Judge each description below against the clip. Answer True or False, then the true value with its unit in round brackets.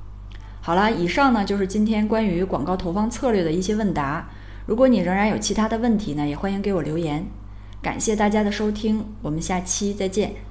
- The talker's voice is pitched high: True (195 Hz)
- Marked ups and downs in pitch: True (5.9 semitones)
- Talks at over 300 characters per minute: True (310 characters per minute)